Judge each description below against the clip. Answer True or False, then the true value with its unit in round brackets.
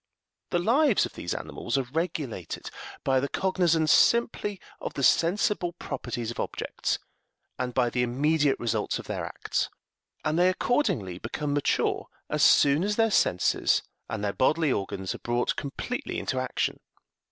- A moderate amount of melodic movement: False (6.6 semitones)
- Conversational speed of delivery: True (150 wpm)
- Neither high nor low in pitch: True (145 Hz)